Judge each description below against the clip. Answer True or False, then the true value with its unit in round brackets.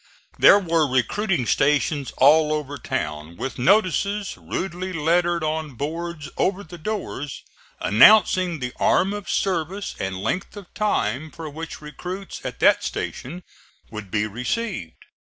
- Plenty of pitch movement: True (5.8 semitones)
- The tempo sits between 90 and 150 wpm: True (135 wpm)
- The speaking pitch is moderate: True (160 Hz)